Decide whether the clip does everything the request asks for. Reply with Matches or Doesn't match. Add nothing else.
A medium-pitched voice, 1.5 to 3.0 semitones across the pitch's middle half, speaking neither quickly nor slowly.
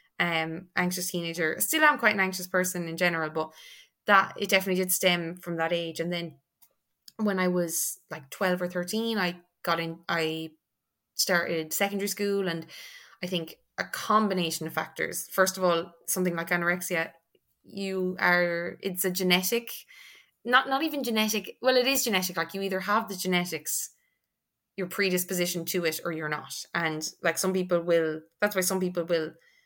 Matches